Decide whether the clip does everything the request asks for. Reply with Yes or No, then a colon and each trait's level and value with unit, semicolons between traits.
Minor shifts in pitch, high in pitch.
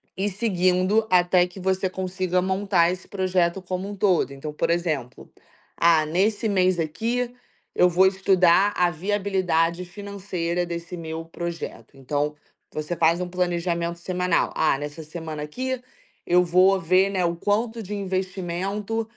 No: narrow, 2.2 semitones; medium, 180 Hz